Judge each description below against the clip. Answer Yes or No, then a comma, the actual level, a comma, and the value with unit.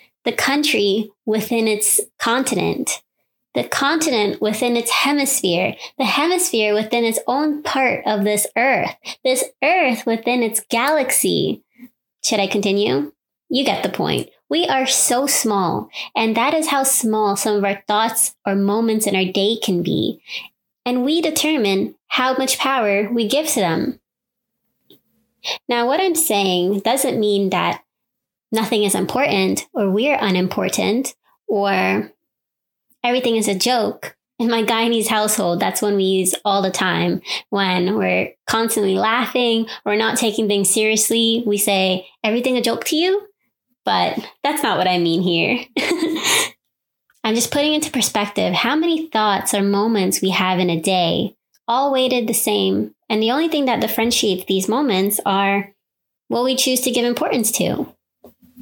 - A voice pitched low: No, high, 225 Hz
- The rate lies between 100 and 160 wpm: Yes, average, 150 wpm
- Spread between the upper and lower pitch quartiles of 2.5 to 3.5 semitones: No, average, 4.4 semitones